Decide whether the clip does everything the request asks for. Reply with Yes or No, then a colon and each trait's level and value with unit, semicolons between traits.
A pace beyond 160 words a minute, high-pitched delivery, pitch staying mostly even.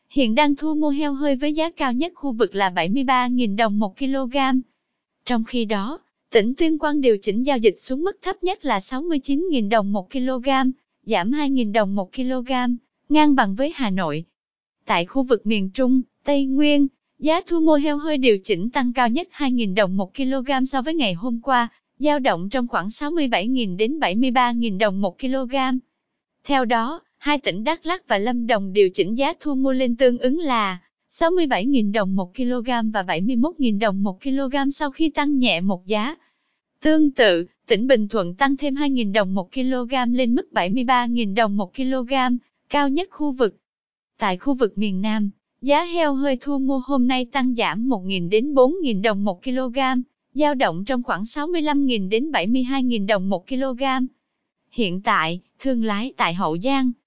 No: average, 180 wpm; very high, 255 Hz; average, 4.3 semitones